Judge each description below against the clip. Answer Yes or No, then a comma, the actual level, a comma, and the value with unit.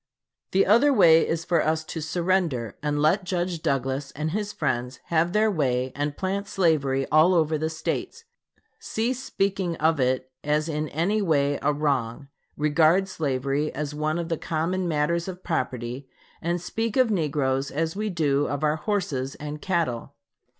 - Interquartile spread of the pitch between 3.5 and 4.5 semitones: Yes, average, 4.0 semitones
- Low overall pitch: No, medium, 155 Hz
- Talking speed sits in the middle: Yes, average, 165 wpm